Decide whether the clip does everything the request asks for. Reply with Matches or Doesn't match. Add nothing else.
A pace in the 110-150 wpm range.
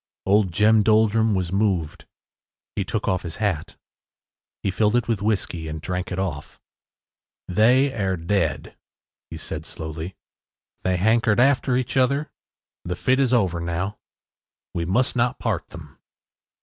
Matches